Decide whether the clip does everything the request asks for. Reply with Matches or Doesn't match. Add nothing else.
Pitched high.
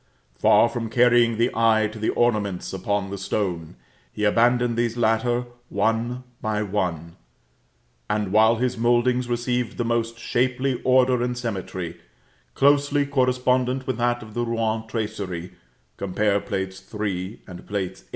Doesn't match